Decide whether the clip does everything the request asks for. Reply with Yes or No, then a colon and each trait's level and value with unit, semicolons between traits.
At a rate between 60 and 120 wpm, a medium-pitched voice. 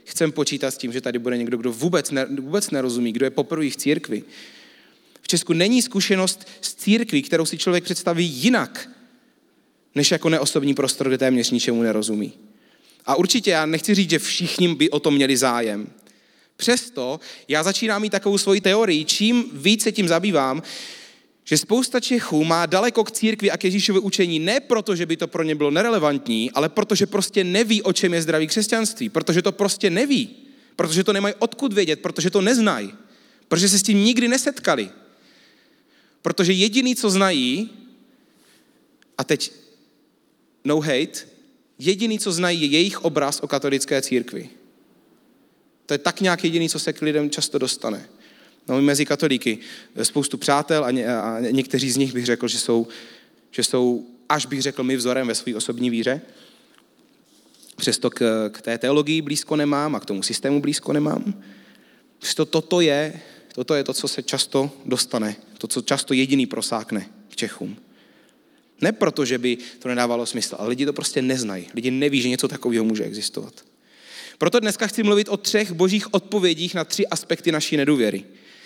No: fast, 170 wpm; medium, 160 Hz